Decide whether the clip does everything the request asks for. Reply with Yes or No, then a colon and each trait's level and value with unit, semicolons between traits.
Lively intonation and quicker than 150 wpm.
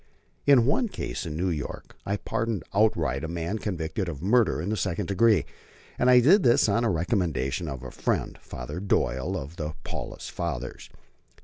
Yes: wide, 6.2 semitones; average, 180 wpm